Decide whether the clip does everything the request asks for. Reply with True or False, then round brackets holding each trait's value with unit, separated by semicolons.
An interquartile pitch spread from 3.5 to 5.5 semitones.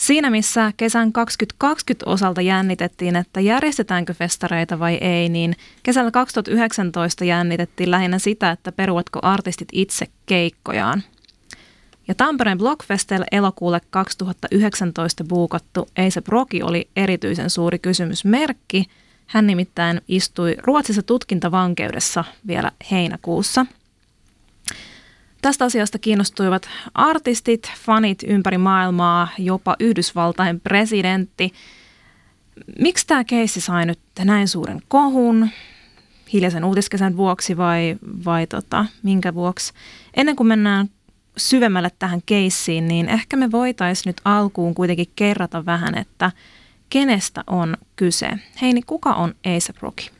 True (4.0 semitones)